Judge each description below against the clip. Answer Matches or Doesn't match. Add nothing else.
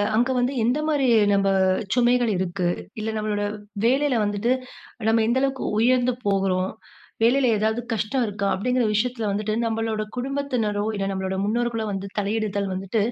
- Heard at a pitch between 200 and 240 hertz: Matches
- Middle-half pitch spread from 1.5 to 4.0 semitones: Matches